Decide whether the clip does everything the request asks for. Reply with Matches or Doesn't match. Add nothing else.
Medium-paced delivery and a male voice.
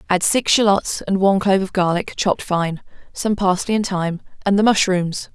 Doesn't match